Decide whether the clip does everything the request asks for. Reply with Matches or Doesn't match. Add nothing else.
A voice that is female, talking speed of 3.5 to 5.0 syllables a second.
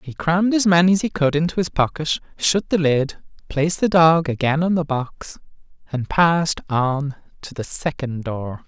Doesn't match